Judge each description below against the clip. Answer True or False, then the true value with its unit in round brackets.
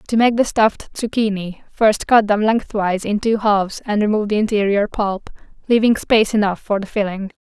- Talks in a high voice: True (210 Hz)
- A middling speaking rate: True (185 wpm)